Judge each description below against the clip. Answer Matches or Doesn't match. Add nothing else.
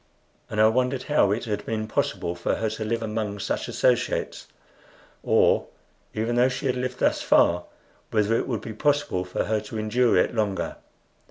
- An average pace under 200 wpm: Matches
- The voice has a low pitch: Matches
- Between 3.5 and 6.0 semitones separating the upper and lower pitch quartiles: Doesn't match